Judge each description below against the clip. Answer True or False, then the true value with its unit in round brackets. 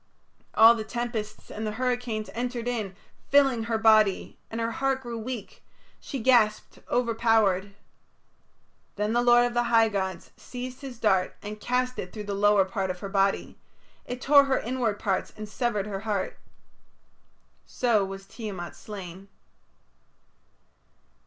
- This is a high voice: True (220 Hz)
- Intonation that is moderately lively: True (3.1 semitones)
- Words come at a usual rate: True (145 wpm)